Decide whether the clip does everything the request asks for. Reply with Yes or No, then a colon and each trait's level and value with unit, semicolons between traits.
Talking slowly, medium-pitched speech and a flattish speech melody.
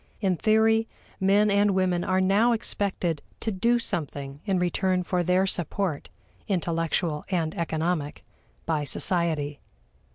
No: slow, 125 wpm; medium, 180 Hz; average, 3.5 semitones